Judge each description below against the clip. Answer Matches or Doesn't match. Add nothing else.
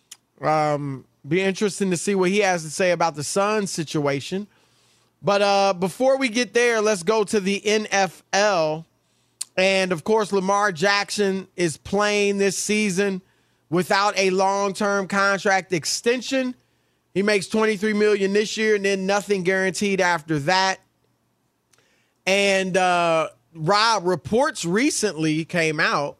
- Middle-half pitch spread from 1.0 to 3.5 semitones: Matches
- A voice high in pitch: Matches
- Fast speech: Doesn't match